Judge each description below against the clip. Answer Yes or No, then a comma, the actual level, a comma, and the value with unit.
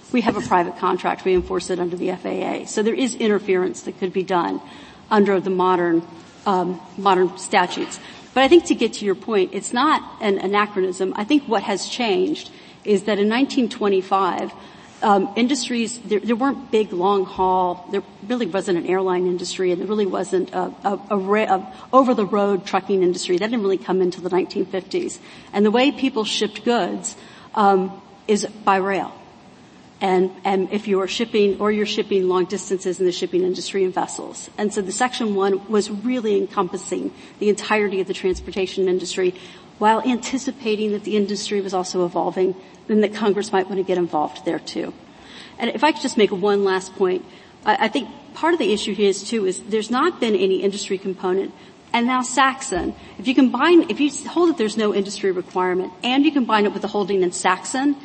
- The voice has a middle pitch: No, high, 200 Hz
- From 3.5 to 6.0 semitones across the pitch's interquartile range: No, average, 3.1 semitones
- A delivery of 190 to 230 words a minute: Yes, average, 195 wpm